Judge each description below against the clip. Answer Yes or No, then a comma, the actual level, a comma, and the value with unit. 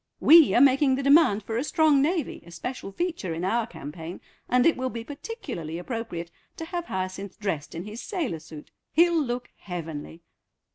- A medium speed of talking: Yes, average, 180 wpm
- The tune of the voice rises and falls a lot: Yes, wide, 9.0 semitones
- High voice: Yes, high, 235 Hz